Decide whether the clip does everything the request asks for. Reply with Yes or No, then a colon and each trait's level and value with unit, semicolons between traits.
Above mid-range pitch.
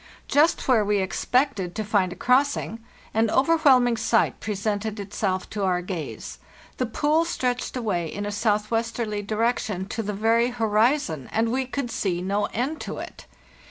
Yes: high, 220 Hz